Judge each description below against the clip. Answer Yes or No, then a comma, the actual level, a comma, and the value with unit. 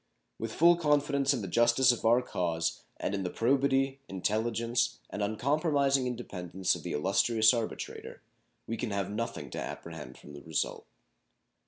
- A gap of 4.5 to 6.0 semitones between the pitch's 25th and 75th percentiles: Yes, wide, 5.6 semitones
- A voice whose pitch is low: Yes, low, 115 Hz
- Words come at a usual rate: Yes, average, 155 wpm